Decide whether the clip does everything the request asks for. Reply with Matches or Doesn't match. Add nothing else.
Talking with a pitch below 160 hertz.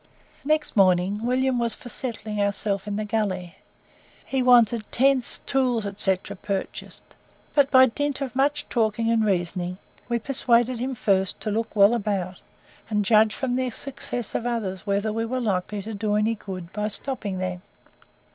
Doesn't match